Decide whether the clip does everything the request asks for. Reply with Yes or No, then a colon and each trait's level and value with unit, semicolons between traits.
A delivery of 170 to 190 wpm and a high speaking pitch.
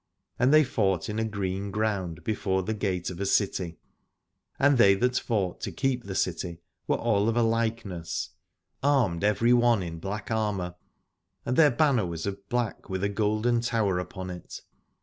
No: average, 175 wpm; low, 105 Hz